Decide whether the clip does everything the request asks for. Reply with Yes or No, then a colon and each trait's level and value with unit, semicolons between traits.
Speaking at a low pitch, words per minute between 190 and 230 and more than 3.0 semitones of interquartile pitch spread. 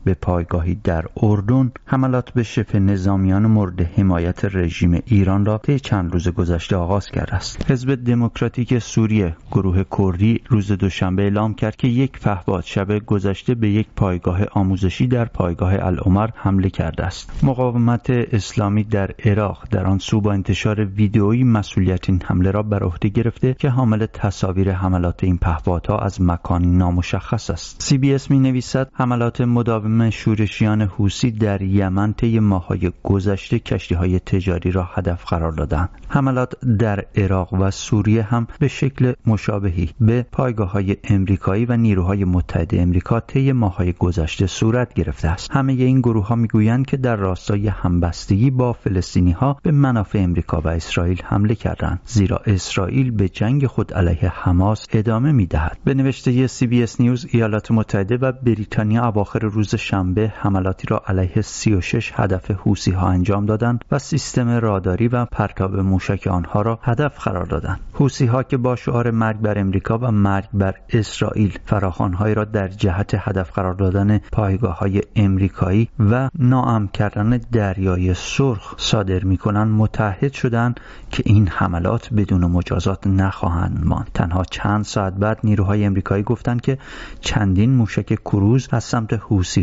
No: low, 105 Hz; average, 150 wpm; average, 3.7 semitones